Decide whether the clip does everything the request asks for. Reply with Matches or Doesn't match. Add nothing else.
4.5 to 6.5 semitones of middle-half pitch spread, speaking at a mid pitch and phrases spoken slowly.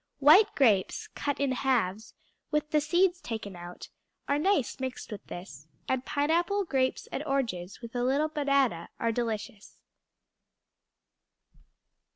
Doesn't match